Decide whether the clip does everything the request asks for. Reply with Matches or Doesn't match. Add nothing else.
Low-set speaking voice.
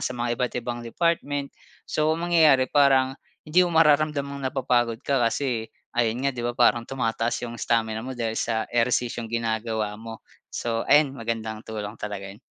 Matches